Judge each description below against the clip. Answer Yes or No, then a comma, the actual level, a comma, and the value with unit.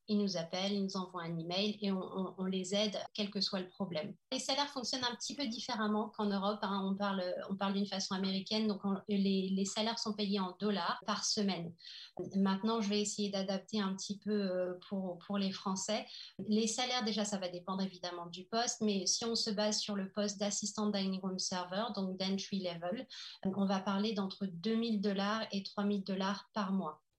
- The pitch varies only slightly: Yes, narrow, 1.8 semitones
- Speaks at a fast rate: No, average, 210 wpm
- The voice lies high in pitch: Yes, high, 200 Hz